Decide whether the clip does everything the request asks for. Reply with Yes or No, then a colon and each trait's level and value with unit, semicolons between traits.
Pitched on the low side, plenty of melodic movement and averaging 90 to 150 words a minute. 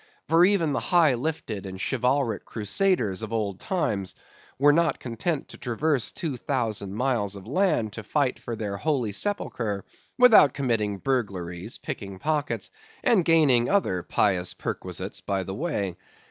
Yes: low, 120 Hz; wide, 7.2 semitones; average, 145 wpm